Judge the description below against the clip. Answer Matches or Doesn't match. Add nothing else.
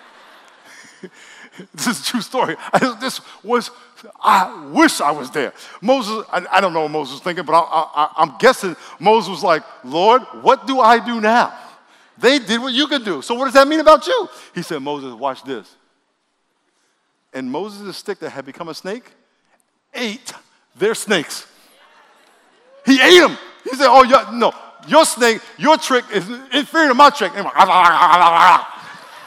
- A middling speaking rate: Matches